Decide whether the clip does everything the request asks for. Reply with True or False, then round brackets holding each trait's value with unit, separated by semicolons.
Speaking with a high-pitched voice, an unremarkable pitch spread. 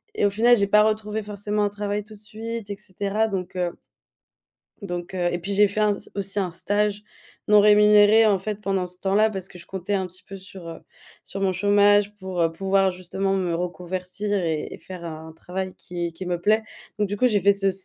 False (195 Hz; 2.3 semitones)